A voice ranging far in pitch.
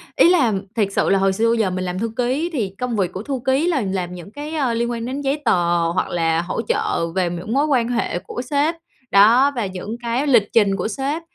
Yes: wide, 6.1 semitones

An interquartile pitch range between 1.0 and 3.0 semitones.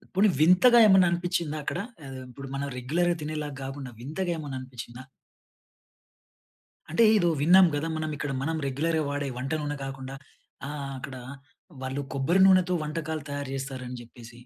No: average, 4.1 semitones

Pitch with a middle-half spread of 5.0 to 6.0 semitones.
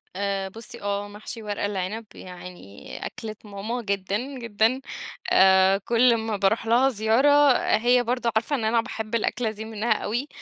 No: average, 2.8 semitones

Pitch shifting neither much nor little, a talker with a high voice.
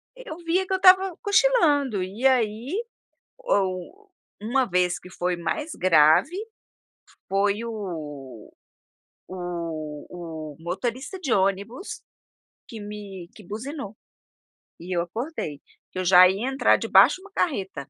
No: wide, 8.5 semitones; high, 205 Hz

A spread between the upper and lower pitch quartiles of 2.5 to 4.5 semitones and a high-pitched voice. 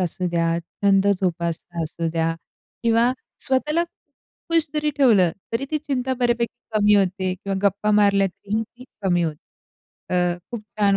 No: average, 5.1 semitones; high, 200 Hz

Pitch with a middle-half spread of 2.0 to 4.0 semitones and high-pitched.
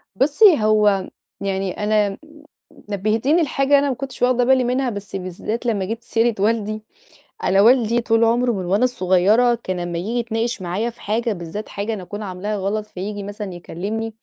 Yes: average, 3.5 semitones; high, 215 Hz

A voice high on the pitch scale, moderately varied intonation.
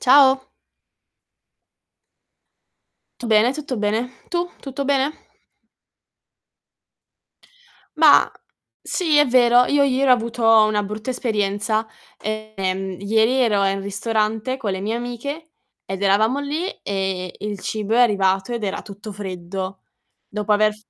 Yes: high, 220 Hz; average, 4.0 semitones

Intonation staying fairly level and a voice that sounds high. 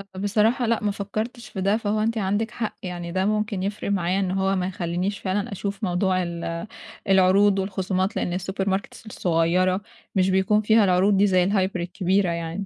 Yes: narrow, 2.0 semitones; high, 195 Hz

